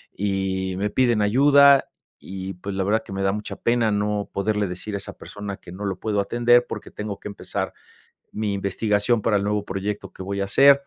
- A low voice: Yes, low, 105 Hz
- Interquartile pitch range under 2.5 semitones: Yes, narrow, 2.0 semitones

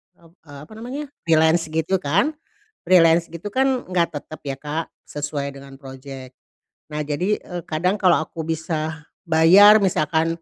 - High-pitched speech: No, medium, 160 Hz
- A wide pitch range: No, average, 3.4 semitones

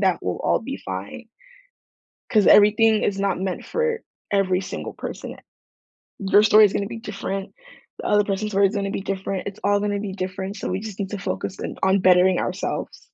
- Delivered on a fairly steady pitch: Yes, narrow, 1.6 semitones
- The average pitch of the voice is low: No, high, 195 Hz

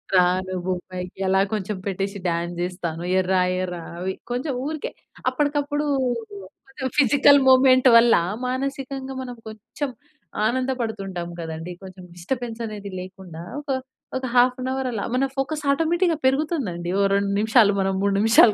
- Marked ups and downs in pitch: Yes, wide, 6.2 semitones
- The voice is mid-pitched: No, high, 220 Hz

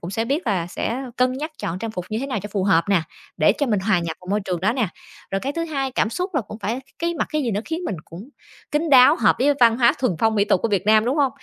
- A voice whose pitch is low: No, high, 225 Hz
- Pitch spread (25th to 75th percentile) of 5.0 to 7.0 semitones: Yes, wide, 5.6 semitones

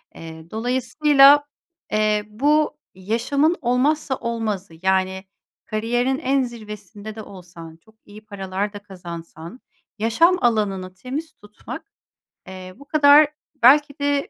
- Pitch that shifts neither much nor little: No, wide, 6.4 semitones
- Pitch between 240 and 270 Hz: No, high, 220 Hz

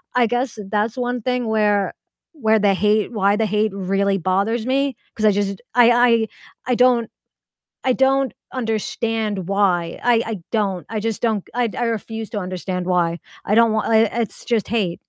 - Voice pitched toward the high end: Yes, high, 220 Hz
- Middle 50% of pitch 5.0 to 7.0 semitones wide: No, average, 2.9 semitones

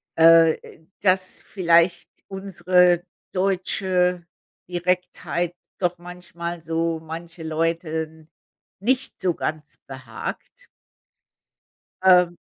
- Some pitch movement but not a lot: No, narrow, 1.9 semitones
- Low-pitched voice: No, medium, 175 Hz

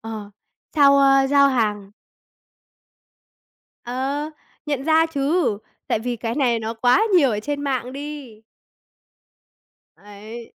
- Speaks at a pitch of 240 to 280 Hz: Yes, very high, 260 Hz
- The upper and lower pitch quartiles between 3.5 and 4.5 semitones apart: Yes, average, 4.1 semitones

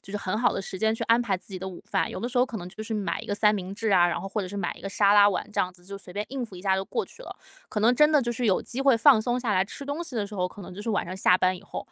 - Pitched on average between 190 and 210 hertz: Yes, high, 205 Hz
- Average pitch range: Yes, average, 3.8 semitones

